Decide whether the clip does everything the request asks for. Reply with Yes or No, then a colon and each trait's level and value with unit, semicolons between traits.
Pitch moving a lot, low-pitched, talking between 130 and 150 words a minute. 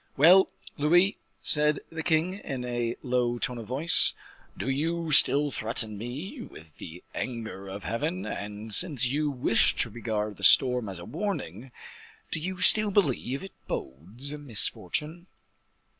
Yes: wide, 6.2 semitones; low, 130 Hz; average, 145 wpm